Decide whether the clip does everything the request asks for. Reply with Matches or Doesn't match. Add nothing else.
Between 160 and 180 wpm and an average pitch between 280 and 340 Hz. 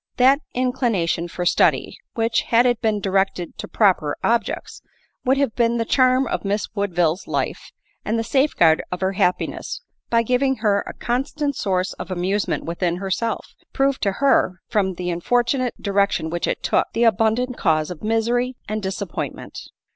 Doesn't match